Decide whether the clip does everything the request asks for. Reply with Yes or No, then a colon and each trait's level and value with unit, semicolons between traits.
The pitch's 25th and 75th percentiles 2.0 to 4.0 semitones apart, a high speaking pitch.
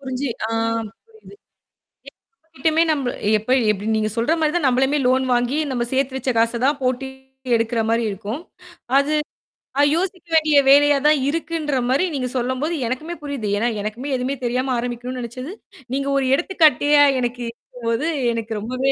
Yes: average, 3.6 semitones; very high, 260 Hz